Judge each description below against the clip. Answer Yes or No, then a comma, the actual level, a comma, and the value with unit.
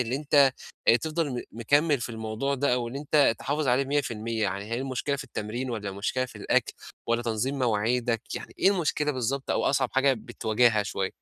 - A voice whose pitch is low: Yes, low, 125 Hz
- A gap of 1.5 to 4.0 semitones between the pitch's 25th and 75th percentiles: Yes, average, 3.5 semitones